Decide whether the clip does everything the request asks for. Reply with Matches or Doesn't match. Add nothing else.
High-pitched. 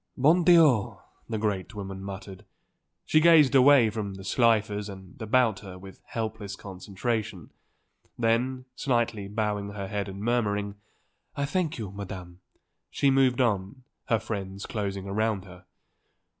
Doesn't match